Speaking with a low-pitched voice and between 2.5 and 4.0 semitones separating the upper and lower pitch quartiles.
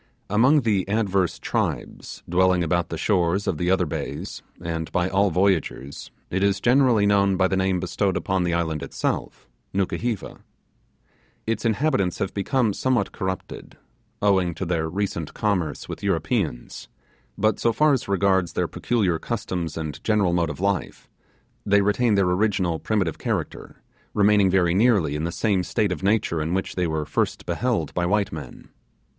Yes: very low, 95 Hz; average, 3.1 semitones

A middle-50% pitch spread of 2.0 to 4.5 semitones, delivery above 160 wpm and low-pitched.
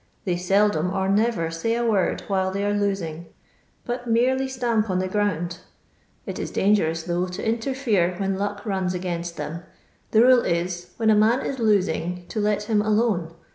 No: average, 3.8 semitones; average, 175 wpm; high, 200 Hz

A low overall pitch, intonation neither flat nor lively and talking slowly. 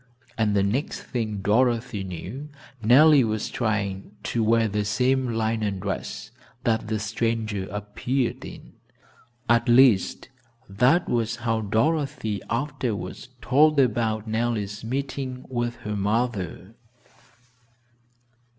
Yes: low, 115 Hz; average, 3.3 semitones; slow, 110 wpm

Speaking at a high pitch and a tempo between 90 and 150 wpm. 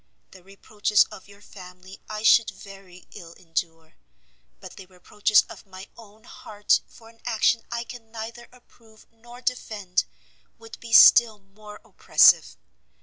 Yes: high, 210 Hz; average, 145 wpm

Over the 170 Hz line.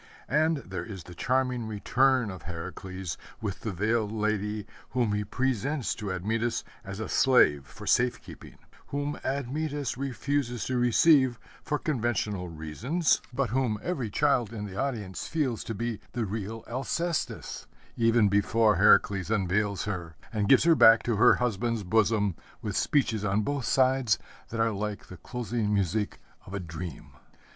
No: low, 110 Hz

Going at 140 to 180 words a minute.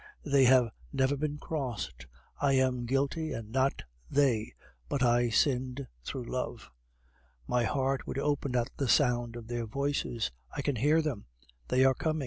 Yes: average, 160 wpm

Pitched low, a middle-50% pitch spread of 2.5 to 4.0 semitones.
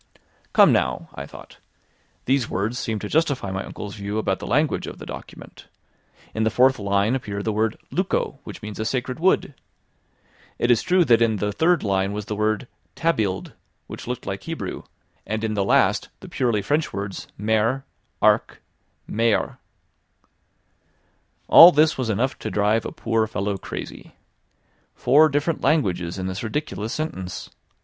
No: low, 110 Hz; average, 4.7 semitones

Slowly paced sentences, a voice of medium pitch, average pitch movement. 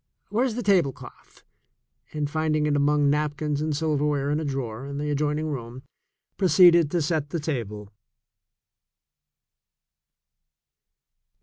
No: slow, 120 wpm; medium, 150 Hz; narrow, 1.9 semitones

